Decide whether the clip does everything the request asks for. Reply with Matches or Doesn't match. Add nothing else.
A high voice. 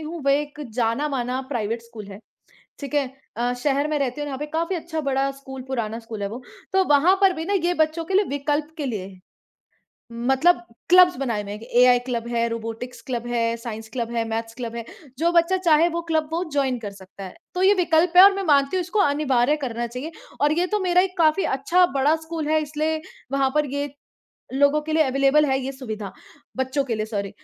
Matches